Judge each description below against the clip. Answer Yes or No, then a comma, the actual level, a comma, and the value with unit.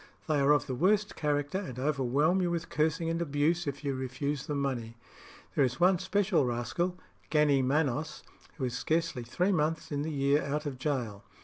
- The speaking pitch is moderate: Yes, medium, 145 Hz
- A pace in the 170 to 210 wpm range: Yes, average, 190 wpm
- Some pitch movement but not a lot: Yes, average, 3.7 semitones